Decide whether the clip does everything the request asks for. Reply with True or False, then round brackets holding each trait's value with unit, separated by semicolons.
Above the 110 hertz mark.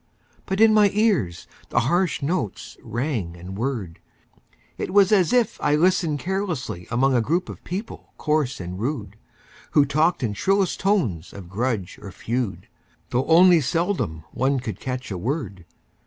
True (135 Hz)